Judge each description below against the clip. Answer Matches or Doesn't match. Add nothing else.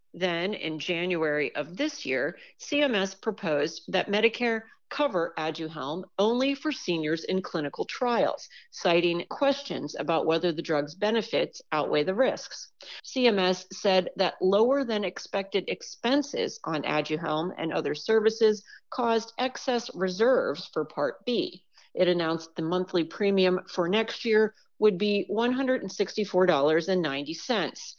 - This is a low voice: Doesn't match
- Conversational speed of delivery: Doesn't match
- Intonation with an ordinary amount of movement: Matches